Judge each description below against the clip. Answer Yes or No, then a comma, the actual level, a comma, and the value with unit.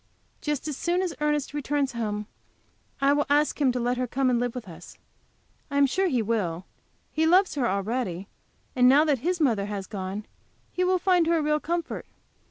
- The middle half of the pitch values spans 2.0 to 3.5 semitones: No, average, 5.2 semitones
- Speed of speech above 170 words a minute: Yes, average, 200 wpm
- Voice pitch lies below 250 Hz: No, very high, 270 Hz